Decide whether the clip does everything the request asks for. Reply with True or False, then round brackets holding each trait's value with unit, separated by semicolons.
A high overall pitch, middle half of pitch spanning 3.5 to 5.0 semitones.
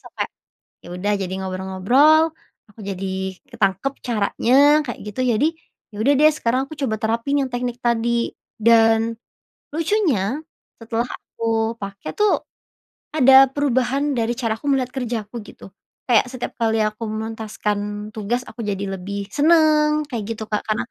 True (230 Hz; 3.9 semitones)